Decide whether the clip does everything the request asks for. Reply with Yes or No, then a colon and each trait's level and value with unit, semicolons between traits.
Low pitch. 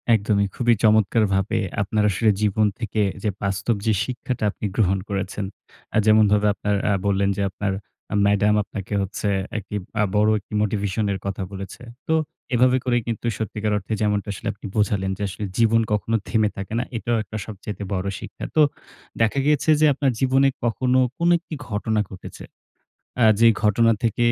Yes: low, 105 Hz